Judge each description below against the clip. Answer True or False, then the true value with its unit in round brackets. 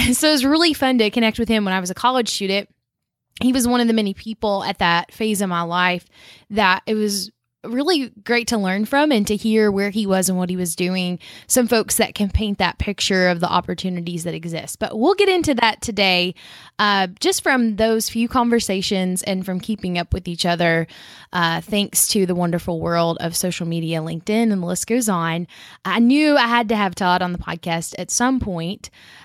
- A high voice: True (200 Hz)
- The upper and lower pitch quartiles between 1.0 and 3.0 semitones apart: False (4.4 semitones)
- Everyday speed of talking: False (215 wpm)